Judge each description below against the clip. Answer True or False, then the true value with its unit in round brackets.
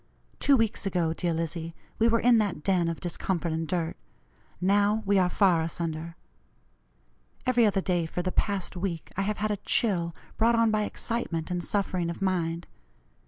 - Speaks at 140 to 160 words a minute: False (175 wpm)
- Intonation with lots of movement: False (3.8 semitones)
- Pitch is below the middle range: False (185 Hz)